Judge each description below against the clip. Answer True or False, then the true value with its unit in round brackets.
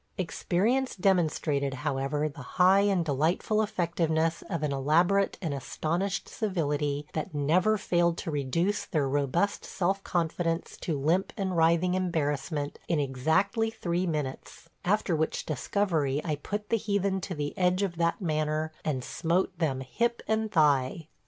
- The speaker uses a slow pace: False (145 wpm)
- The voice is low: False (165 Hz)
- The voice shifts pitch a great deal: False (4.4 semitones)